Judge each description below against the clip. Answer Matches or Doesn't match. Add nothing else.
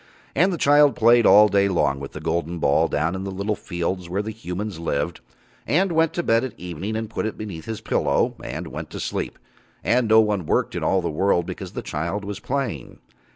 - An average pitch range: Matches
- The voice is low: Matches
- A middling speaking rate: Doesn't match